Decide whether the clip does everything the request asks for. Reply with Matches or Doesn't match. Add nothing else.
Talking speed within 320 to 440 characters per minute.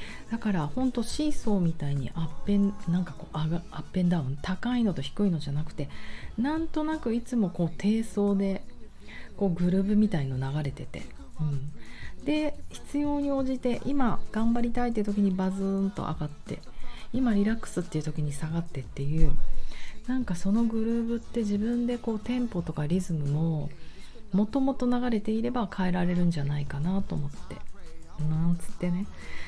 Matches